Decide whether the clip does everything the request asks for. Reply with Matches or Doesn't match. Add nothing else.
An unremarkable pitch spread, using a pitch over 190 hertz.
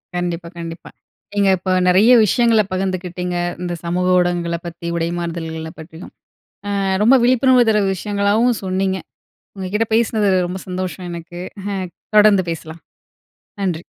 Doesn't match